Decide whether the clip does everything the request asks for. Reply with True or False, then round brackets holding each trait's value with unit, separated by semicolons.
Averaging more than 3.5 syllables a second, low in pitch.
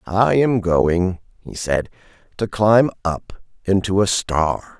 False (3.3 syllables/s; 95 Hz)